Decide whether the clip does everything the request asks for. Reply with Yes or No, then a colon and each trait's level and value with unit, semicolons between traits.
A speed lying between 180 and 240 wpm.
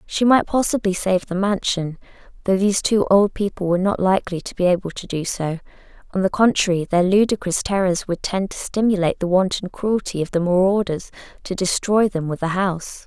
Yes: average, 190 wpm